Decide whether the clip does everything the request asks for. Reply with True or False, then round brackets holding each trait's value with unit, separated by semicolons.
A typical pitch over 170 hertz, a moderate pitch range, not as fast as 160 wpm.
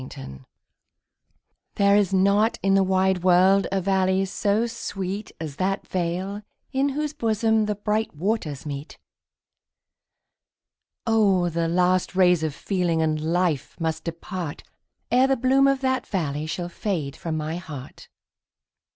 True (190 Hz; 3.8 semitones; 135 wpm)